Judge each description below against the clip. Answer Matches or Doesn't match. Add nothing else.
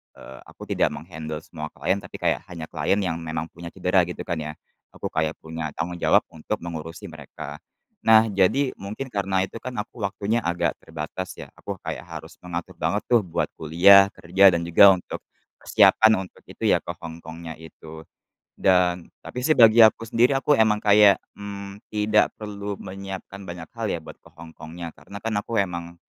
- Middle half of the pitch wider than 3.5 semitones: Matches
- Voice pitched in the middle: Doesn't match